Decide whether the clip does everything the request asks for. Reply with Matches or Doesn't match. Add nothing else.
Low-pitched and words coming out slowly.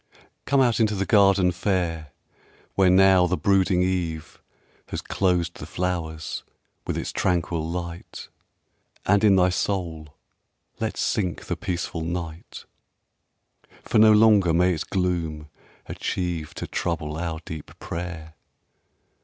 Matches